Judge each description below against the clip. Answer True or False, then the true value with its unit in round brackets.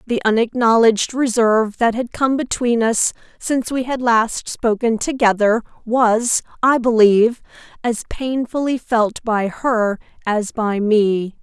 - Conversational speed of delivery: False (130 wpm)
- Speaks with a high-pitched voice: True (230 Hz)